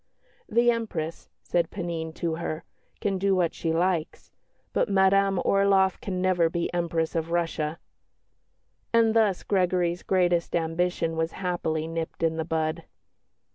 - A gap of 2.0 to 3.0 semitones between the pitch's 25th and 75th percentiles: Yes, average, 2.7 semitones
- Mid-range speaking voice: Yes, medium, 175 Hz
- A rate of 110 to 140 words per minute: Yes, slow, 135 wpm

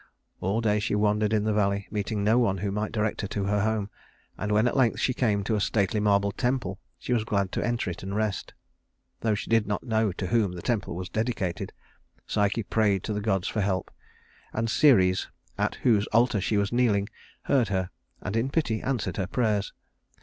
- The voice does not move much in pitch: Yes, narrow, 2.2 semitones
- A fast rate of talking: Yes, fast, 210 wpm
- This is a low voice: Yes, low, 105 Hz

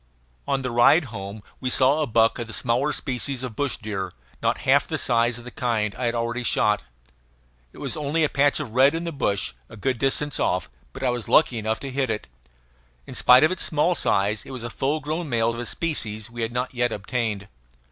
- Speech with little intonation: No, average, 3.7 semitones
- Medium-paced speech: No, fast, 230 wpm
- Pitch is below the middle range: Yes, low, 120 Hz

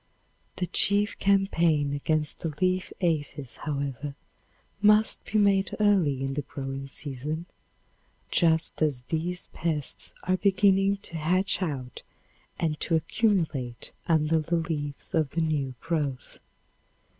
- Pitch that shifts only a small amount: No, average, 4.3 semitones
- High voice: No, medium, 160 Hz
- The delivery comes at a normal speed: No, slow, 120 wpm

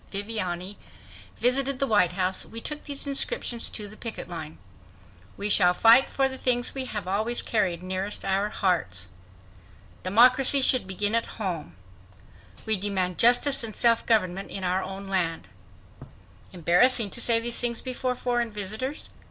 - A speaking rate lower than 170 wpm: Yes, average, 150 wpm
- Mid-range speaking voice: No, high, 210 Hz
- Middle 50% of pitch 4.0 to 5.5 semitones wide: Yes, average, 4.5 semitones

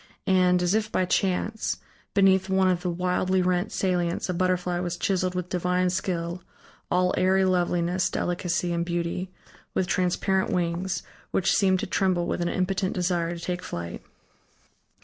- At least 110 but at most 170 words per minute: Yes, average, 155 wpm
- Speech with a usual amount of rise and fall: No, narrow, 1.2 semitones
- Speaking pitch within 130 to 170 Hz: No, medium, 180 Hz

